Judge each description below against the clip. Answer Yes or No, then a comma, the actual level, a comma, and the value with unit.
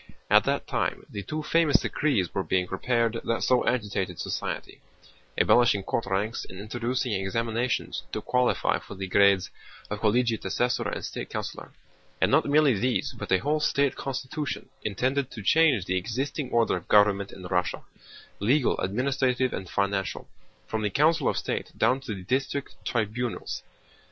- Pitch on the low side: Yes, low, 115 Hz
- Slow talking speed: No, average, 155 wpm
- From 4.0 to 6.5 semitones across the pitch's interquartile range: Yes, average, 4.9 semitones